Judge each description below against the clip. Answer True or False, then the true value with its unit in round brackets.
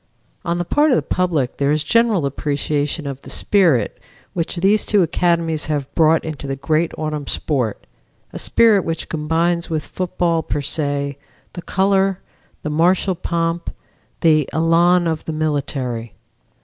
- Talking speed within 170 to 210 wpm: False (150 wpm)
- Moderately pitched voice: True (160 Hz)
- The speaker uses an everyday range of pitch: True (3.2 semitones)